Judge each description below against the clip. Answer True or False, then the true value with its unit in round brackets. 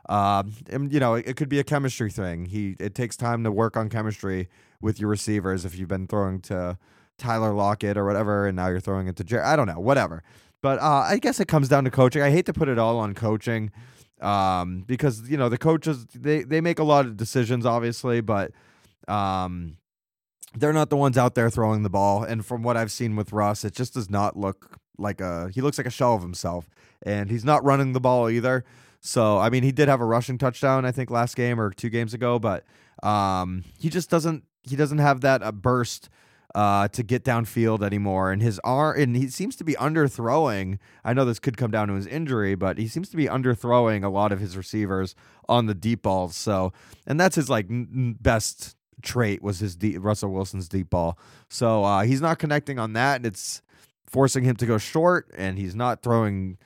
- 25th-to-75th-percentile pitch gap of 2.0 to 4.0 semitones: False (4.4 semitones)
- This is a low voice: True (115 Hz)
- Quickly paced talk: True (220 wpm)